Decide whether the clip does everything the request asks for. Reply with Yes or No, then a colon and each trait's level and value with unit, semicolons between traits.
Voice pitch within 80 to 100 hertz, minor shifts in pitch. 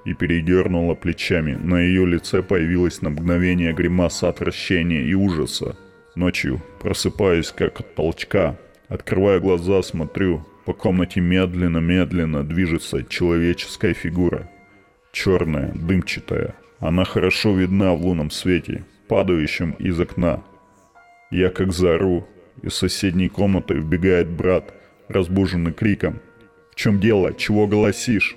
Yes: very low, 90 Hz; narrow, 1.8 semitones